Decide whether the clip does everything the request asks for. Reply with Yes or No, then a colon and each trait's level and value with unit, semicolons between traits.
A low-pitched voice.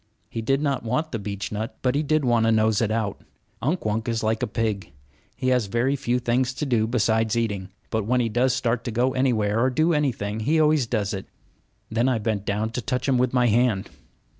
Yes: low, 115 Hz